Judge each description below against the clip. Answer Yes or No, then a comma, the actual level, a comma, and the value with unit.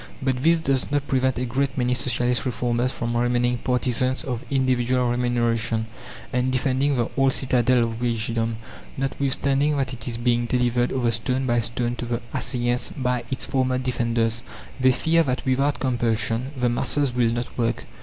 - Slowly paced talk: No, average, 165 wpm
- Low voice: Yes, low, 125 Hz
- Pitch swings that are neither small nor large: No, narrow, 1.7 semitones